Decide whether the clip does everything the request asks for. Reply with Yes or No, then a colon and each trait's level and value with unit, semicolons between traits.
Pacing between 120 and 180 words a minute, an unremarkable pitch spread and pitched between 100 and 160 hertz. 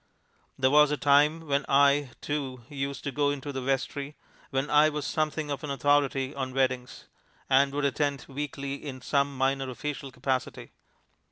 No: average, 165 wpm; narrow, 1.5 semitones; medium, 140 Hz